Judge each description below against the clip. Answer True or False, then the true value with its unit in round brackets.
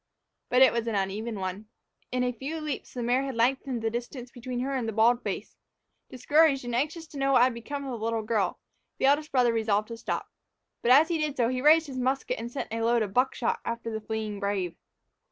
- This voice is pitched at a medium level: False (245 Hz)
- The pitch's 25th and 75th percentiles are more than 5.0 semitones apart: False (3.2 semitones)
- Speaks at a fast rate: True (230 wpm)